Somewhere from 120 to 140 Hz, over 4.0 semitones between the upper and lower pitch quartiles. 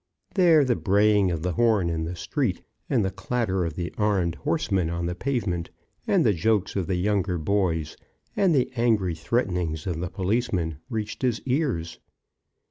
No: very low, 95 Hz; average, 5.3 semitones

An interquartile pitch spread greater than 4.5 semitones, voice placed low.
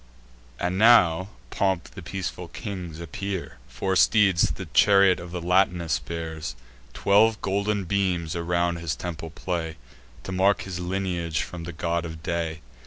No: narrow, 2.5 semitones; very low, 90 Hz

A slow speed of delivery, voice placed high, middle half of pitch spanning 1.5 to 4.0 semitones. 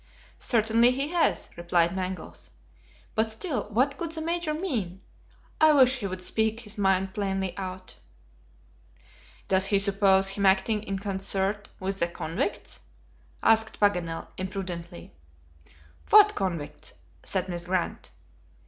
Yes: slow, 125 wpm; high, 195 Hz; average, 3.5 semitones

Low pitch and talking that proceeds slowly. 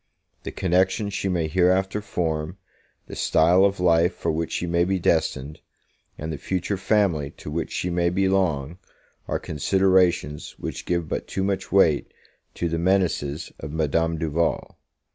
No: very low, 85 Hz; average, 155 wpm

